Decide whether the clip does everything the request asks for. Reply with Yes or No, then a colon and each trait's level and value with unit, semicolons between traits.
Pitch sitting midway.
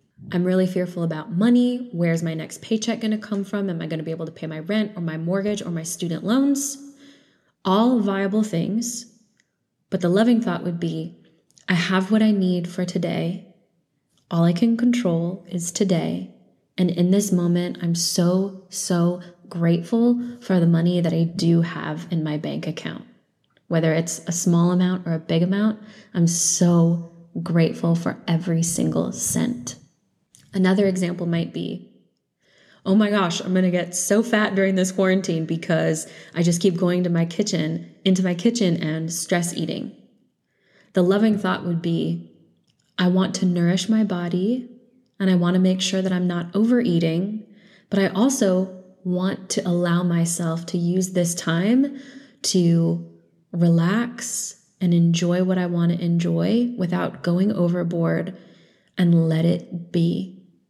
Yes: medium, 180 Hz